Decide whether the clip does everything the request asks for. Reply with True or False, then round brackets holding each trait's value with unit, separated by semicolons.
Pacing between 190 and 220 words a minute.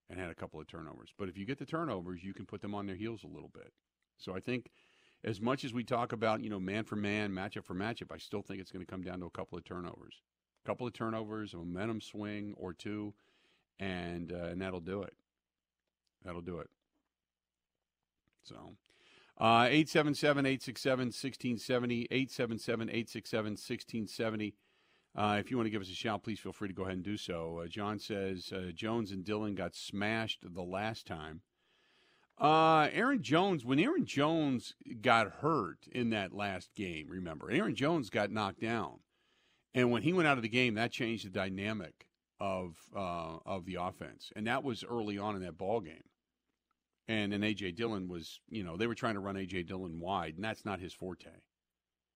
True (195 wpm)